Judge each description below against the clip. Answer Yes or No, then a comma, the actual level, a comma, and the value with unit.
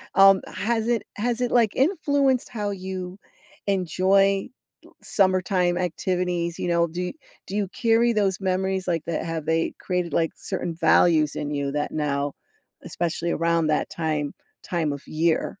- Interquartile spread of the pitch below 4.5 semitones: Yes, average, 3.2 semitones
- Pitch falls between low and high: Yes, medium, 180 Hz